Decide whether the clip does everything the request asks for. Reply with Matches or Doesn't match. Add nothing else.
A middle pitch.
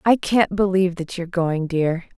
Matches